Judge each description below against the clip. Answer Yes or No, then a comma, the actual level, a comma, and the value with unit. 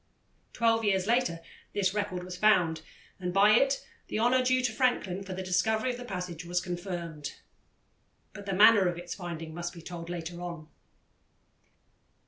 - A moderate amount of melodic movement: Yes, average, 3.7 semitones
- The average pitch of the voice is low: No, medium, 185 Hz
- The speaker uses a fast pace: No, average, 165 wpm